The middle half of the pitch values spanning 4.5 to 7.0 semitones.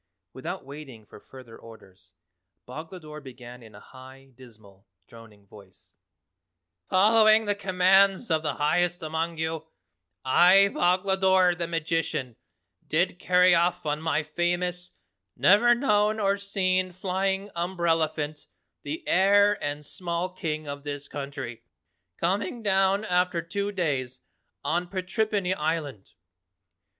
Yes: average, 4.9 semitones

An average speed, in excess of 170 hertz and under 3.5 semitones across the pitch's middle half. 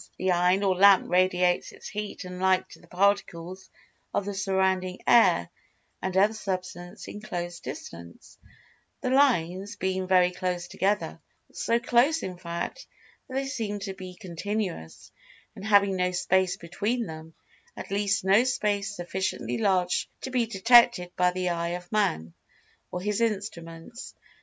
Yes: average, 145 wpm; high, 190 Hz; average, 2.7 semitones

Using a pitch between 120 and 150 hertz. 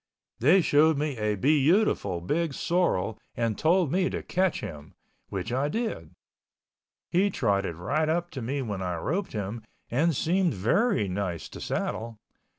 Yes: low, 135 Hz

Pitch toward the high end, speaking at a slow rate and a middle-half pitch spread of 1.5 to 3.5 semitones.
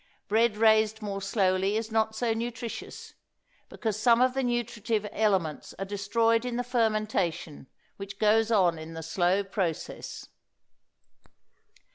Yes: high, 215 Hz; slow, 130 wpm; average, 2.8 semitones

